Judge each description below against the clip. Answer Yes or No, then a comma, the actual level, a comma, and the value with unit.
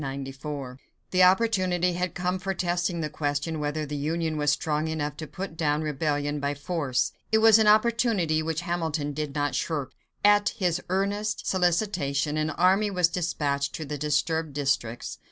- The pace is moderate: Yes, average, 160 wpm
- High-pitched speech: No, medium, 160 Hz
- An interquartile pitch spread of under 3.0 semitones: No, average, 3.8 semitones